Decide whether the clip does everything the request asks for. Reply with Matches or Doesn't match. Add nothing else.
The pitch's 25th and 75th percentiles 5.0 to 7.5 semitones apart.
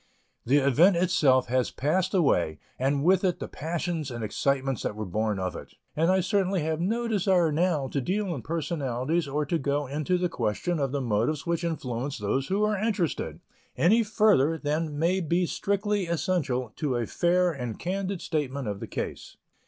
Matches